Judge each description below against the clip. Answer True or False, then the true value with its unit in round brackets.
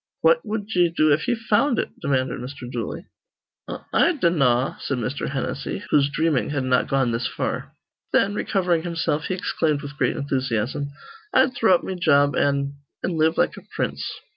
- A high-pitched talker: False (150 Hz)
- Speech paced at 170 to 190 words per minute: True (180 wpm)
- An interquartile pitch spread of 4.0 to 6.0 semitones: True (4.8 semitones)